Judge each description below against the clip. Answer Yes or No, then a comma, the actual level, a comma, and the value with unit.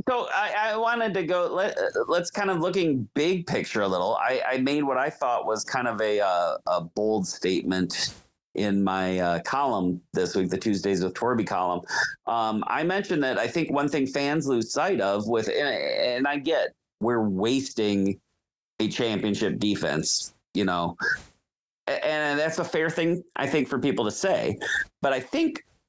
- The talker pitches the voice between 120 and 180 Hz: Yes, medium, 140 Hz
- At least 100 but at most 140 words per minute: No, average, 185 wpm